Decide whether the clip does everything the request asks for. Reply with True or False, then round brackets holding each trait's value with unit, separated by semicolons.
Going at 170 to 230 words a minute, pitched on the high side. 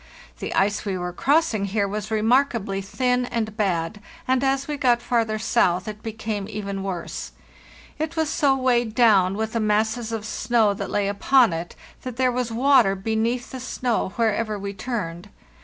True (175 wpm; 220 Hz)